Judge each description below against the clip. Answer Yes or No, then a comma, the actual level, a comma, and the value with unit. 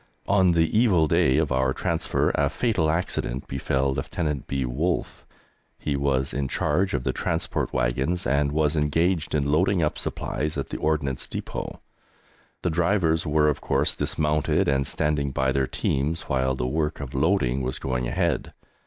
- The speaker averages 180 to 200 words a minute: No, average, 165 wpm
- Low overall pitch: Yes, very low, 75 Hz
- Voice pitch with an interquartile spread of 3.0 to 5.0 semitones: Yes, average, 3.5 semitones